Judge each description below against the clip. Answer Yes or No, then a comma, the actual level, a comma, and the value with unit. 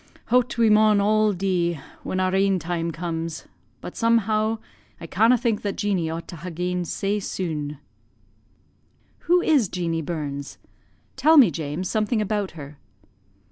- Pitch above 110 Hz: Yes, medium, 185 Hz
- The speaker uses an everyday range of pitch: Yes, average, 4.4 semitones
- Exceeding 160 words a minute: No, average, 145 wpm